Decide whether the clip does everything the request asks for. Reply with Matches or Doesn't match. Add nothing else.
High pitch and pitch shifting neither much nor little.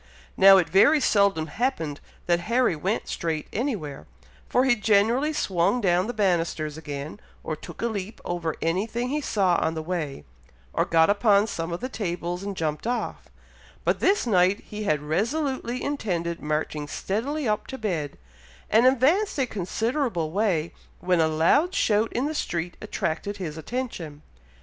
Doesn't match